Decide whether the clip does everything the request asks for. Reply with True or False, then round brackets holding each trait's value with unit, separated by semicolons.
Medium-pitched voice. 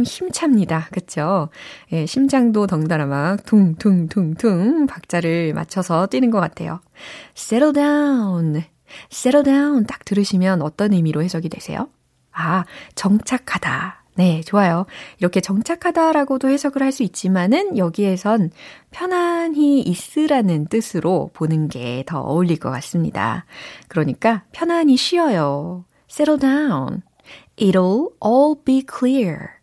False (205 Hz)